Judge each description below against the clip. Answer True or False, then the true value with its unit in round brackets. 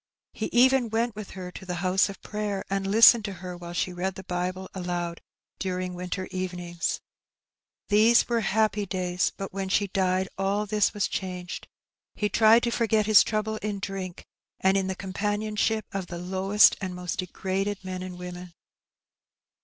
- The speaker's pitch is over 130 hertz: True (190 Hz)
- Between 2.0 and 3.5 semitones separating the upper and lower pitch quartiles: True (2.5 semitones)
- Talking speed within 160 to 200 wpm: True (170 wpm)